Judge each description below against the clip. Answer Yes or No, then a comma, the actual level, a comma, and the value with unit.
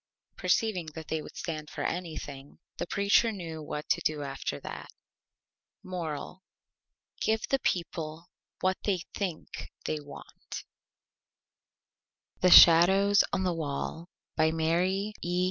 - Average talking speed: No, slow, 125 wpm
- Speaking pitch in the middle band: Yes, medium, 170 Hz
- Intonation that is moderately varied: Yes, average, 3.3 semitones